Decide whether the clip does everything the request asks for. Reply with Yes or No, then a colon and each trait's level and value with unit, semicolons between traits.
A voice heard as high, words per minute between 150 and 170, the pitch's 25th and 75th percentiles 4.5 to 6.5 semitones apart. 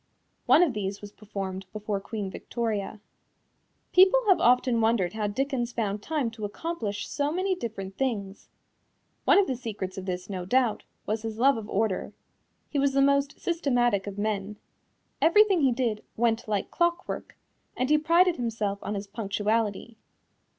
Yes: high, 225 Hz; average, 160 wpm; average, 5.2 semitones